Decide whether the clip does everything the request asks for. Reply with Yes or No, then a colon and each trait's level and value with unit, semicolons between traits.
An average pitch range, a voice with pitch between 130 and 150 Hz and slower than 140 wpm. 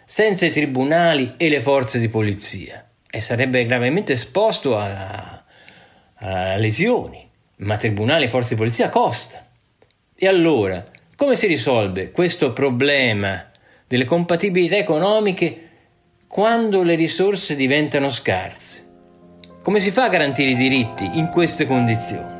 No: wide, 7.8 semitones; low, 135 Hz; average, 125 wpm